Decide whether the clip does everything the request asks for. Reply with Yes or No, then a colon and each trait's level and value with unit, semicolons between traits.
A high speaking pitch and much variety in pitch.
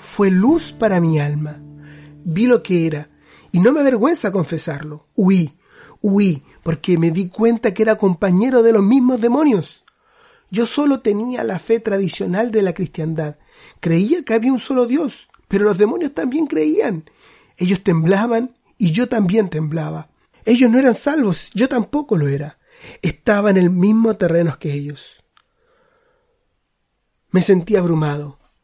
Yes: high, 200 Hz; wide, 6.7 semitones